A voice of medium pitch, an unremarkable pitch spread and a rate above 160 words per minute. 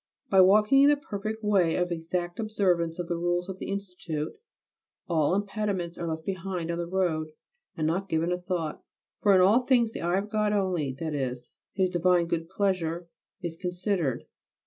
Yes: medium, 180 Hz; average, 3.0 semitones; average, 185 wpm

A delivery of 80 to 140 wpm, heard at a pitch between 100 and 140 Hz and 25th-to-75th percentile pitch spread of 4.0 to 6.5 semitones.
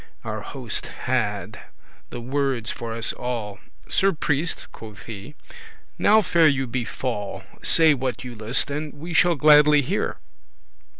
Yes: slow, 135 wpm; low, 135 Hz; average, 4.6 semitones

